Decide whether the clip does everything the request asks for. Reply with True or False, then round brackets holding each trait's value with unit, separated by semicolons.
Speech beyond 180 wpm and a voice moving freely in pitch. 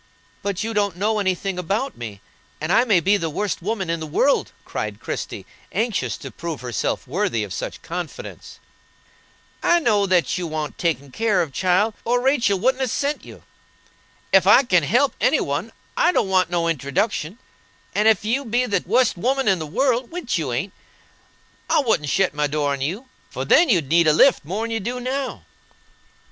True (190 wpm; 6.1 semitones)